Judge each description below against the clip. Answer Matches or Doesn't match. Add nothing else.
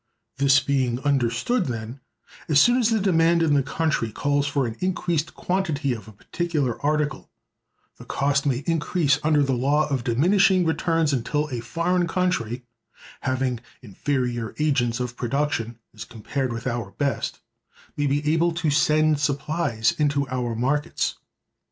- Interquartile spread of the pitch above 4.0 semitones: Matches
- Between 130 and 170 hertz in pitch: Matches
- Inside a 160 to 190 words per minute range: Doesn't match